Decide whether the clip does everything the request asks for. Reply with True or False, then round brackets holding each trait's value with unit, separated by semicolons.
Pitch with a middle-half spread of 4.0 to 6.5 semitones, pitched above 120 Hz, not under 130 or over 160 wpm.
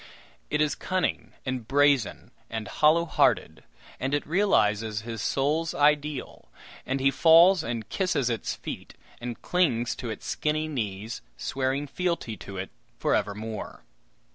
True (5.4 semitones; 135 Hz; 140 wpm)